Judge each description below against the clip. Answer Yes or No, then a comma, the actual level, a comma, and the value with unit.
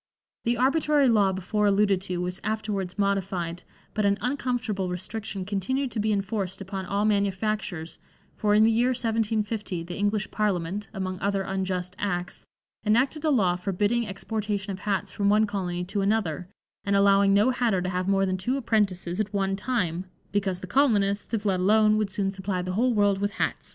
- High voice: Yes, high, 200 Hz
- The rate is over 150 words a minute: Yes, average, 180 wpm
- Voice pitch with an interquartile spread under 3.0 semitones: Yes, narrow, 2.4 semitones